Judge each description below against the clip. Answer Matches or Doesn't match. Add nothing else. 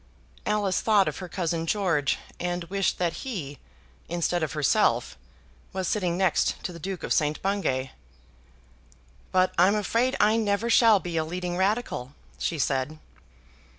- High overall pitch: Doesn't match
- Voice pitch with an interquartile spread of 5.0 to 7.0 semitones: Doesn't match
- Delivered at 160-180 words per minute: Doesn't match